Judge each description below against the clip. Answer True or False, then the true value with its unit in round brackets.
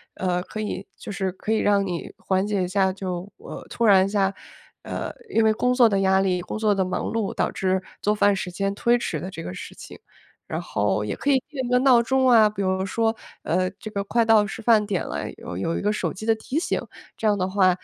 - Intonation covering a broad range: False (2.9 semitones)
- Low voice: False (200 Hz)